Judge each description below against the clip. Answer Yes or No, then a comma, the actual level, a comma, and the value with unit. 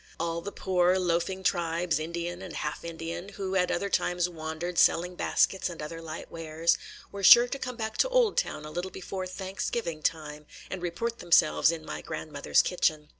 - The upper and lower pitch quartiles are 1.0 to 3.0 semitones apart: Yes, narrow, 2.6 semitones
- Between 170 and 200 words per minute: Yes, average, 175 wpm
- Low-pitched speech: No, medium, 175 Hz